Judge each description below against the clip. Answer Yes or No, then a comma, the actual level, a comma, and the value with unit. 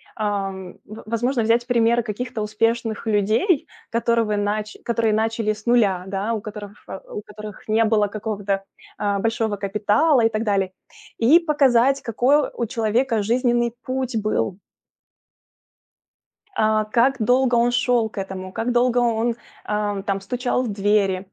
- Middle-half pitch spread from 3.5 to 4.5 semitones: No, narrow, 2.6 semitones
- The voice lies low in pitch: No, high, 225 Hz